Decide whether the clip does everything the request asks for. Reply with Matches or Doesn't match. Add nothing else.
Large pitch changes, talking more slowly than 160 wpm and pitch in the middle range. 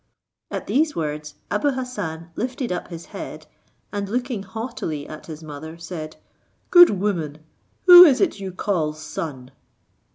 Matches